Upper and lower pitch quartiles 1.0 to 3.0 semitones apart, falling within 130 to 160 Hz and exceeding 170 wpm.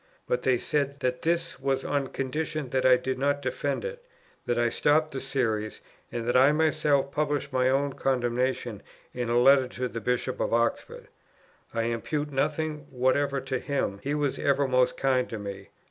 Yes: narrow, 2.6 semitones; low, 135 Hz; average, 180 wpm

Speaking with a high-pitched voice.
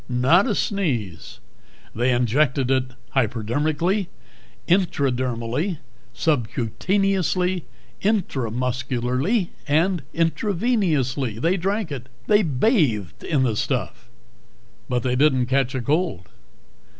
No: low, 135 Hz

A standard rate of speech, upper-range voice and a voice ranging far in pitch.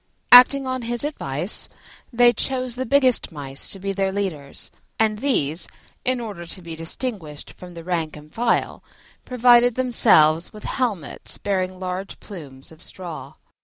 Yes: average, 150 wpm; high, 195 Hz; wide, 6.9 semitones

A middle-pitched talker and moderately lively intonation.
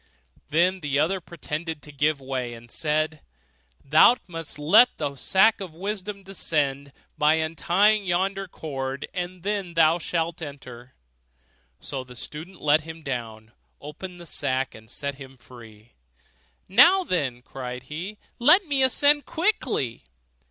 No: medium, 155 Hz; wide, 5.7 semitones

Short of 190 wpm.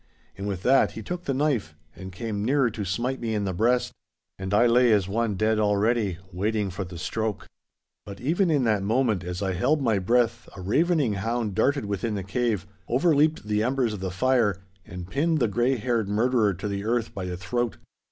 No: fast, 205 wpm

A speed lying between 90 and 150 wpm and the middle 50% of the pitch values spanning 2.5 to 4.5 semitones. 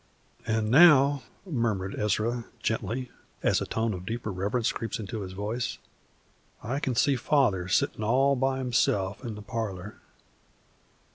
Yes: average, 140 wpm; average, 3.8 semitones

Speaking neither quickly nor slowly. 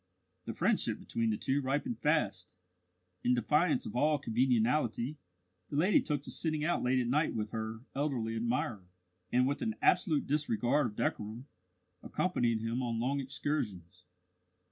Yes: average, 150 wpm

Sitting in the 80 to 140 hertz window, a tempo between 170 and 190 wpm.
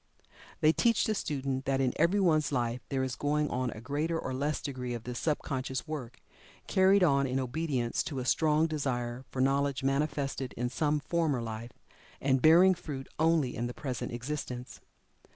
Yes: low, 135 Hz; average, 175 wpm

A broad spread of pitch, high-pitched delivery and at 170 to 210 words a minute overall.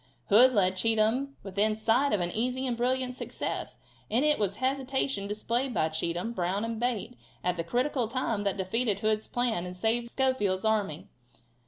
No: average, 4.1 semitones; high, 225 Hz; average, 175 wpm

